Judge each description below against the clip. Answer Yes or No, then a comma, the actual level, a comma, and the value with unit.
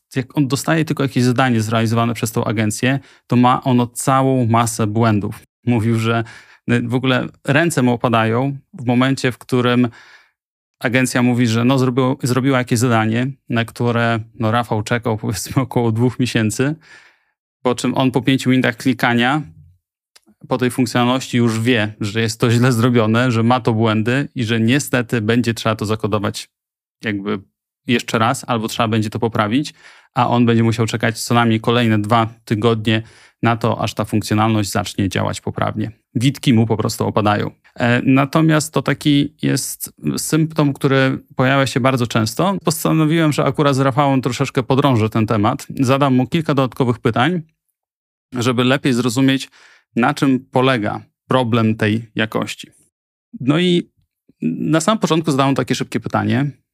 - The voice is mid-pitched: No, low, 125 Hz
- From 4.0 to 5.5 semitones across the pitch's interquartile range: No, average, 2.9 semitones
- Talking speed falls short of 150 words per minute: No, average, 155 wpm